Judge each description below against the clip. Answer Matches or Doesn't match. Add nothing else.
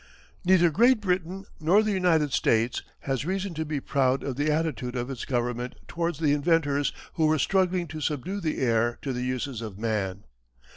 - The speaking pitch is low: Doesn't match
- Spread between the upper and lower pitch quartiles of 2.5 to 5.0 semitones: Doesn't match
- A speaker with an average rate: Matches